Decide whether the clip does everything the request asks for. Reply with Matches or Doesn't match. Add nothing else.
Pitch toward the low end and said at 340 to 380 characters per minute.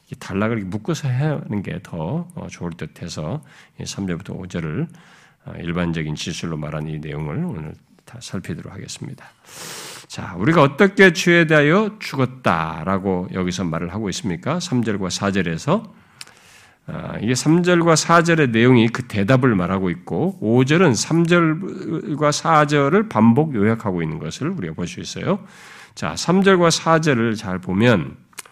Doesn't match